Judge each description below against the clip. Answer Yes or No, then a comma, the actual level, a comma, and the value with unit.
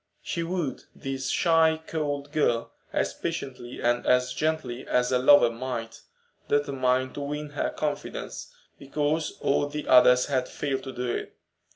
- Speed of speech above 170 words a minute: No, average, 150 wpm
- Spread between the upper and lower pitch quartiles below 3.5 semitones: Yes, average, 2.8 semitones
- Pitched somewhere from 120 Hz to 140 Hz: Yes, low, 135 Hz